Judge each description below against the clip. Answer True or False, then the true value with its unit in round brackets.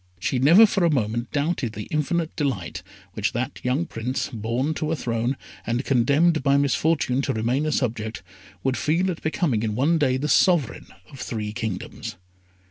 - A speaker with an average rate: True (175 wpm)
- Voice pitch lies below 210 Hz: True (135 Hz)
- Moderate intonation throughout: True (5.0 semitones)